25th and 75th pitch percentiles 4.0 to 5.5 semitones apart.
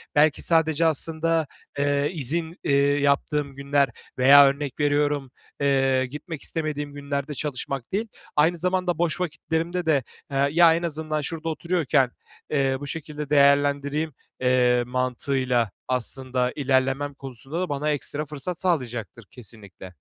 No: average, 2.9 semitones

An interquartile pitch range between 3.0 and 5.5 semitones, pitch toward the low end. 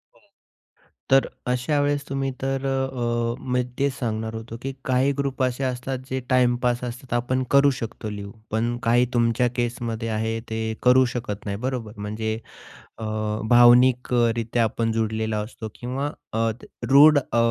No: narrow, 2.5 semitones; low, 120 Hz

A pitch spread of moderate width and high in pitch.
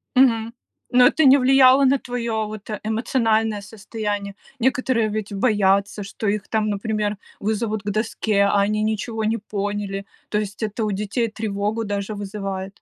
No: narrow, 2.0 semitones; high, 215 Hz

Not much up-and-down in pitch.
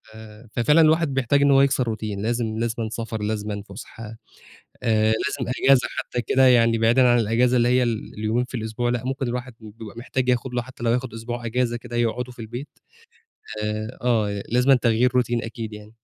Yes: narrow, 2.2 semitones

